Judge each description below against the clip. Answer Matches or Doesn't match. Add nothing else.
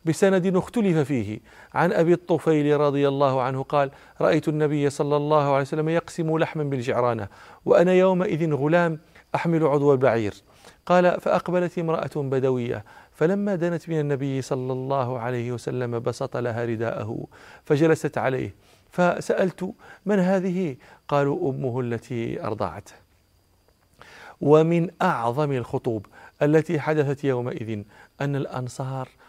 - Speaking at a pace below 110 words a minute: Doesn't match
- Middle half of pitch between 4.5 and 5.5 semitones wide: Matches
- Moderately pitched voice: Matches